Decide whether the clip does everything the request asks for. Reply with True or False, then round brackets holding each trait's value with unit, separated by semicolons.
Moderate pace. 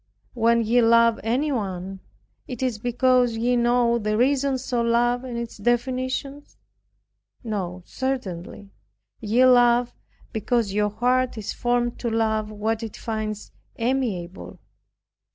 False (120 wpm)